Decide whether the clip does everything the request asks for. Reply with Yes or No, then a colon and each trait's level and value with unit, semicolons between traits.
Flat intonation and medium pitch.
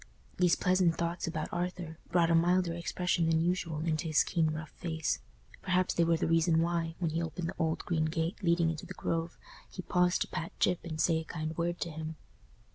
Yes: narrow, 1.4 semitones; medium, 165 Hz